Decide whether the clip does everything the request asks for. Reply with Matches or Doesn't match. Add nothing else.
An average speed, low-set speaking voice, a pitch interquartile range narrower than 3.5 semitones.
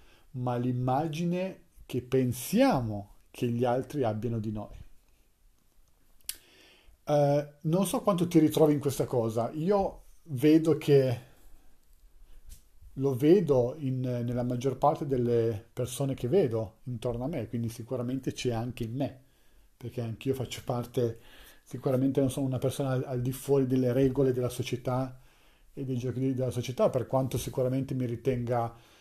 Matches